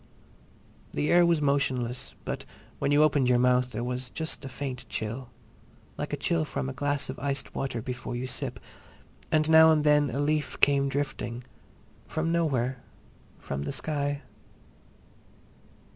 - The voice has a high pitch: No, low, 135 Hz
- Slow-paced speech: No, average, 150 wpm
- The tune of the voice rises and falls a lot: No, average, 2.9 semitones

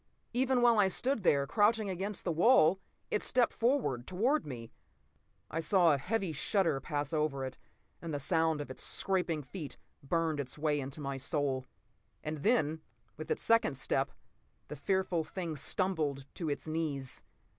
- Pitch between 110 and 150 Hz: No, medium, 160 Hz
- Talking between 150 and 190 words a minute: Yes, average, 165 wpm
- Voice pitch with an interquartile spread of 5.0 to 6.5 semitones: Yes, average, 5.3 semitones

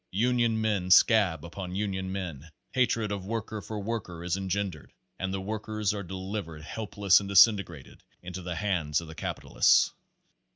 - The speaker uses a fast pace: No, average, 160 wpm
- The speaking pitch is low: Yes, very low, 95 Hz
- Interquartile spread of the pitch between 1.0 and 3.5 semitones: Yes, average, 3.0 semitones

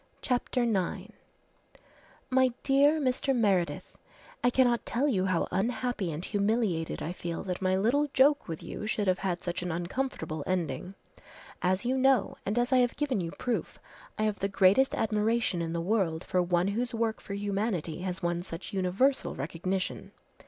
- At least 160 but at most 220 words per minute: Yes, average, 170 wpm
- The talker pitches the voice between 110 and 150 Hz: No, high, 200 Hz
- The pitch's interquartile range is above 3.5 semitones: Yes, wide, 5.4 semitones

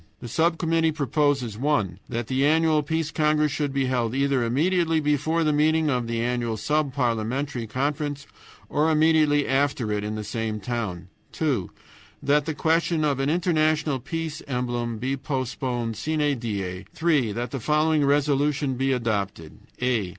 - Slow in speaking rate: No, average, 160 wpm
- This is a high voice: No, medium, 140 Hz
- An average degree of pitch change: Yes, average, 4.4 semitones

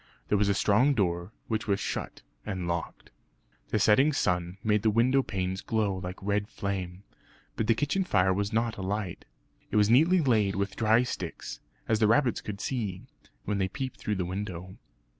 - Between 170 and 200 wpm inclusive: Yes, average, 180 wpm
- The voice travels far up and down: No, average, 3.3 semitones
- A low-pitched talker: Yes, low, 105 Hz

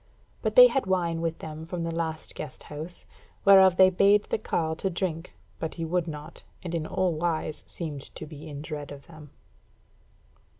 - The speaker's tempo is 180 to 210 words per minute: Yes, average, 185 wpm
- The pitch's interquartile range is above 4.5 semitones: No, narrow, 2.5 semitones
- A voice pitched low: No, medium, 165 Hz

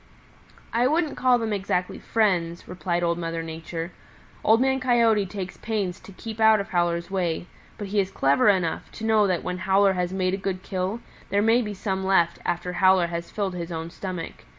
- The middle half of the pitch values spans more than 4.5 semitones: No, average, 3.4 semitones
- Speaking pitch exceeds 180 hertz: Yes, high, 190 Hz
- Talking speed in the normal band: Yes, average, 195 wpm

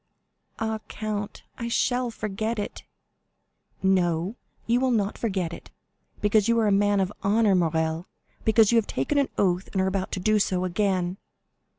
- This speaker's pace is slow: No, average, 170 wpm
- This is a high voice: Yes, high, 205 Hz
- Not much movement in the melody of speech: No, average, 3.0 semitones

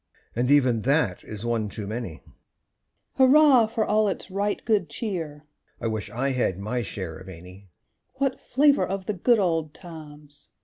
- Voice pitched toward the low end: No, medium, 145 Hz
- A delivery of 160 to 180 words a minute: Yes, average, 165 wpm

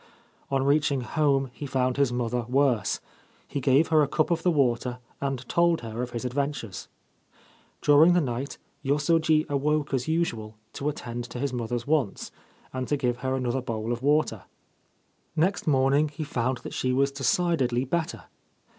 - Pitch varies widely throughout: No, average, 3.4 semitones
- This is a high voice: No, low, 135 Hz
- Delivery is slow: No, average, 165 wpm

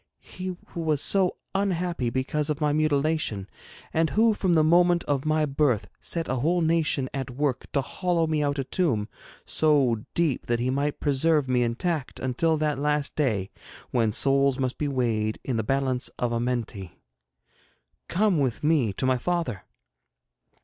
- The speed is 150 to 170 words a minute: Yes, average, 165 wpm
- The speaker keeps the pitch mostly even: No, average, 4.3 semitones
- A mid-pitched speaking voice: Yes, medium, 145 Hz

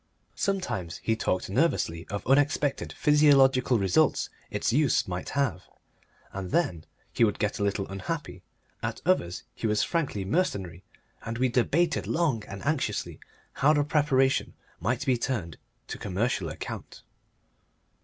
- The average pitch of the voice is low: Yes, low, 120 Hz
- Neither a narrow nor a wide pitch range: No, wide, 7.1 semitones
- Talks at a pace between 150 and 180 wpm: No, slow, 135 wpm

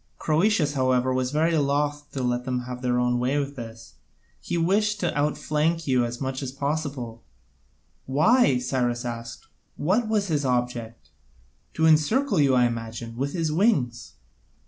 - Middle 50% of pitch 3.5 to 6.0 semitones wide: Yes, average, 4.2 semitones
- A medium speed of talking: Yes, average, 155 wpm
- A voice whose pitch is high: No, low, 135 Hz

